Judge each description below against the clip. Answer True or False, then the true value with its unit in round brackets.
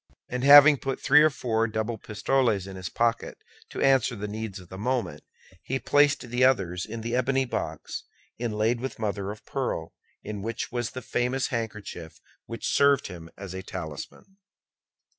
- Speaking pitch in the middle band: False (115 Hz)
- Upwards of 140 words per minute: True (170 wpm)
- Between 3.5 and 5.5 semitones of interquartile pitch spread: True (4.3 semitones)